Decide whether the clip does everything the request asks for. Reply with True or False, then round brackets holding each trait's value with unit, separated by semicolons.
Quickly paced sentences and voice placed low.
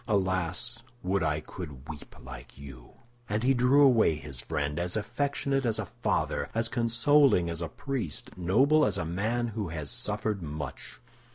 False (165 wpm; 95 Hz)